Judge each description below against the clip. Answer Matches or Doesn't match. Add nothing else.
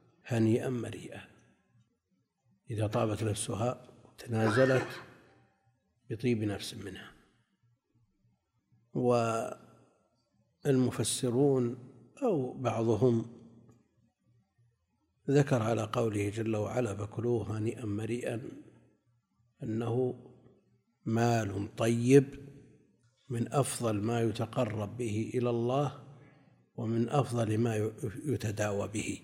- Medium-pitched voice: Doesn't match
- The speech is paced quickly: Doesn't match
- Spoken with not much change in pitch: Matches